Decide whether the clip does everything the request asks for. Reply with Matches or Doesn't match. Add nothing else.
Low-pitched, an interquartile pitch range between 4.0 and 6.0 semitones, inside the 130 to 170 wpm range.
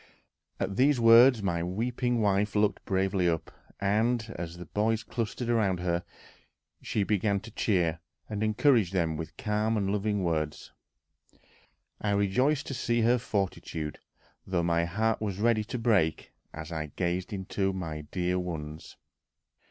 Matches